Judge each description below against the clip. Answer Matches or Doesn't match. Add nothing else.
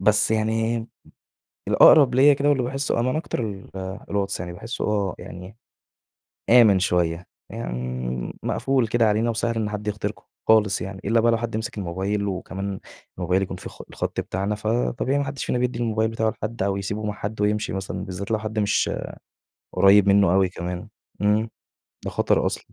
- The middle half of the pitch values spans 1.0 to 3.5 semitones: Matches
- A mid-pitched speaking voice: Doesn't match